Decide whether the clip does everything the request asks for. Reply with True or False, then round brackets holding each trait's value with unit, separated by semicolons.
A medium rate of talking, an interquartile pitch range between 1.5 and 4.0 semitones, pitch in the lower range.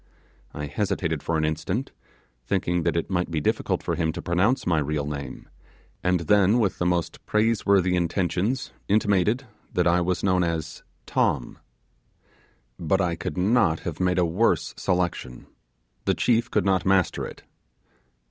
True (155 wpm; 3.0 semitones; 90 Hz)